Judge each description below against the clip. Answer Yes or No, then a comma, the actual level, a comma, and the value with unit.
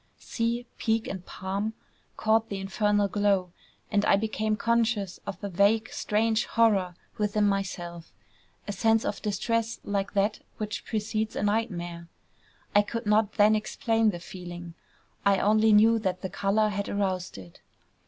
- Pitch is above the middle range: Yes, high, 205 Hz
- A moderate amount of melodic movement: No, narrow, 2.2 semitones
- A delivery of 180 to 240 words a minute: No, average, 150 wpm